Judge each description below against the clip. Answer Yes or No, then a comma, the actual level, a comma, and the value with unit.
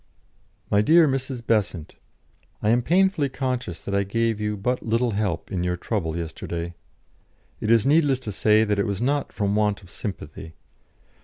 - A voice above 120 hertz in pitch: No, low, 105 Hz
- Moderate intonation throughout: Yes, average, 4.3 semitones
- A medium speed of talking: Yes, average, 170 wpm